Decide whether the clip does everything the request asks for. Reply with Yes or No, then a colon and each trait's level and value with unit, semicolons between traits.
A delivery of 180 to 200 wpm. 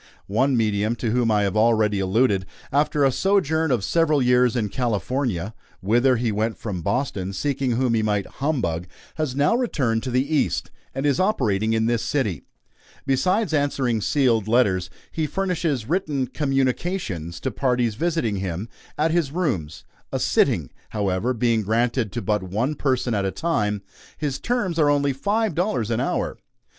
No: average, 165 wpm